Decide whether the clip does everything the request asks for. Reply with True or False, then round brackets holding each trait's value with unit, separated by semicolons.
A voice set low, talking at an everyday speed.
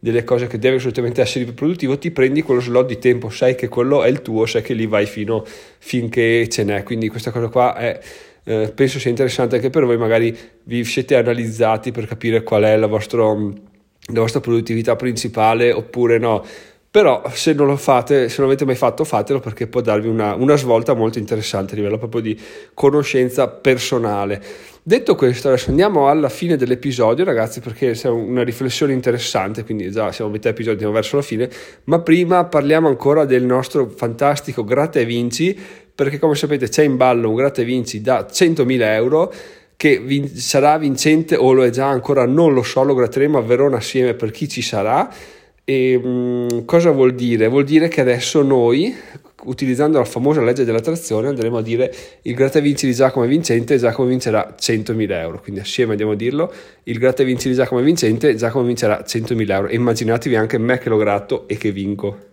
False (125 Hz; 195 wpm)